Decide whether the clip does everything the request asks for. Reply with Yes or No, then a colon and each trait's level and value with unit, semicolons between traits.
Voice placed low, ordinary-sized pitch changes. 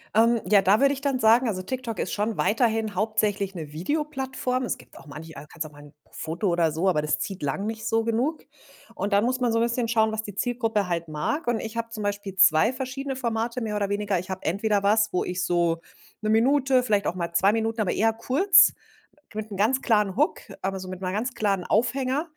No: high, 215 Hz; average, 4.1 semitones